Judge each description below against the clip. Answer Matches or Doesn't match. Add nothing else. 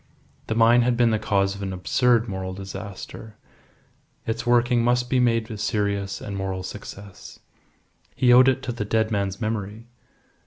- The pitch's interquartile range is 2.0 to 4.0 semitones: Matches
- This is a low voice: Matches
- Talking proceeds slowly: Doesn't match